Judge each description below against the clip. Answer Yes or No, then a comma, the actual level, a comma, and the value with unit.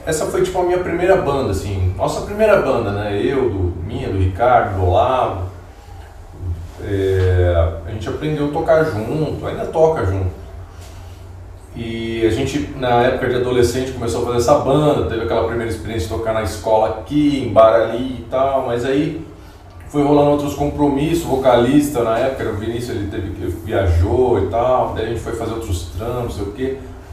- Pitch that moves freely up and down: Yes, wide, 6.0 semitones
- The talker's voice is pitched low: Yes, low, 115 Hz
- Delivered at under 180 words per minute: No, fast, 185 wpm